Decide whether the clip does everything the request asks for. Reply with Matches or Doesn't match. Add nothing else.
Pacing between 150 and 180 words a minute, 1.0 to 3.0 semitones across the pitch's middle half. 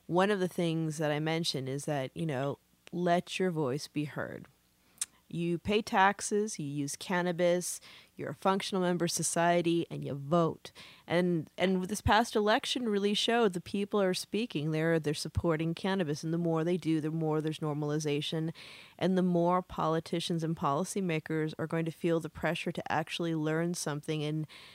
Matches